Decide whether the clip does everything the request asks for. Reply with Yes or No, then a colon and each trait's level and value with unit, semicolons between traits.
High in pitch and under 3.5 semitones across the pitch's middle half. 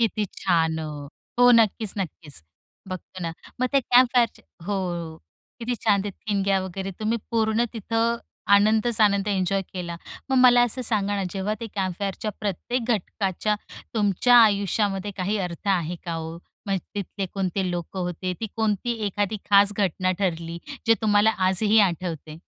Yes: high, 200 Hz; average, 3.0 semitones